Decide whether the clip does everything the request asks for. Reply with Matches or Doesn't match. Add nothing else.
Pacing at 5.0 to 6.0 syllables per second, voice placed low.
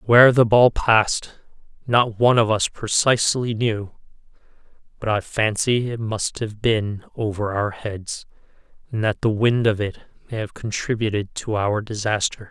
Doesn't match